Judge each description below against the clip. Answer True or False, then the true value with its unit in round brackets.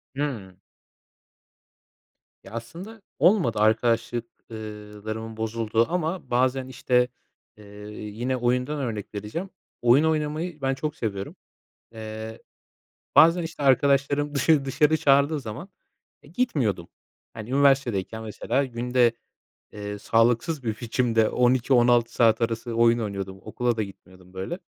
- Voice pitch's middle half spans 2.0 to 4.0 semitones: False (4.4 semitones)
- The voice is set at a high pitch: False (120 Hz)